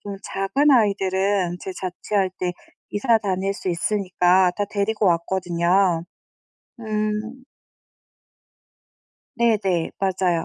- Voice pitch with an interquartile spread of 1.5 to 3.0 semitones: Yes, average, 2.7 semitones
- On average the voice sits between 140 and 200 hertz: Yes, high, 195 Hz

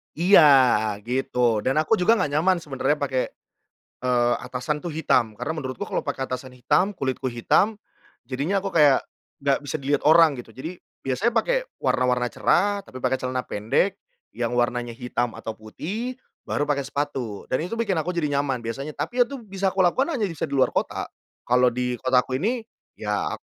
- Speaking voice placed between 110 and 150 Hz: Yes, medium, 140 Hz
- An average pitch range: No, wide, 6.1 semitones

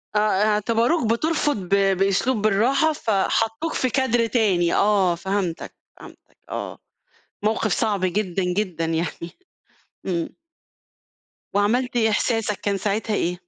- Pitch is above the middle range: Yes, high, 210 Hz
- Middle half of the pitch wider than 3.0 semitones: Yes, average, 3.5 semitones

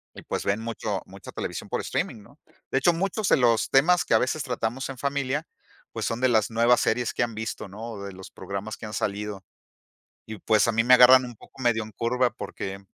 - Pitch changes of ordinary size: Yes, average, 3.2 semitones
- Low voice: Yes, low, 115 Hz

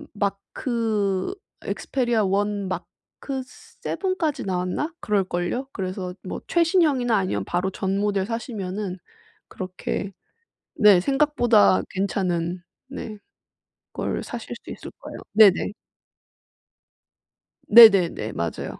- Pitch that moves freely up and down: No, average, 4.3 semitones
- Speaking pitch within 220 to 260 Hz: No, high, 200 Hz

